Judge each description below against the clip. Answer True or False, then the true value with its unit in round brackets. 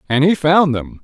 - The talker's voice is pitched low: False (155 Hz)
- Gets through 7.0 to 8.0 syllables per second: False (4.7 syllables/s)